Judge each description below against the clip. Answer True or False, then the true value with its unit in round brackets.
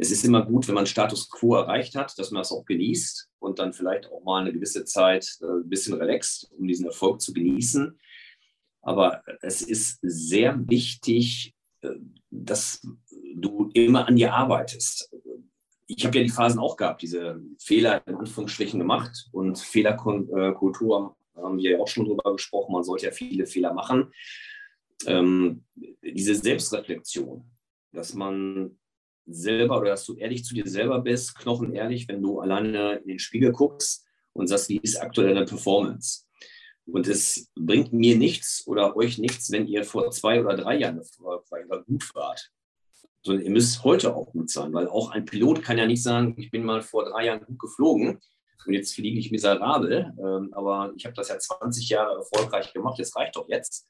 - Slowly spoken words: False (175 wpm)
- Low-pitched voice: True (110 Hz)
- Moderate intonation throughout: True (3.9 semitones)